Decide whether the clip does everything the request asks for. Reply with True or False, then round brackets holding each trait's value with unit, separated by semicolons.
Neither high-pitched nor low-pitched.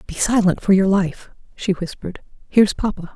False (195 Hz)